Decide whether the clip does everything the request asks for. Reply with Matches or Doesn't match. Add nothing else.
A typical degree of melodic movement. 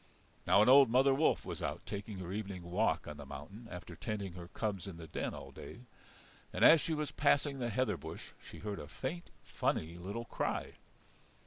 Doesn't match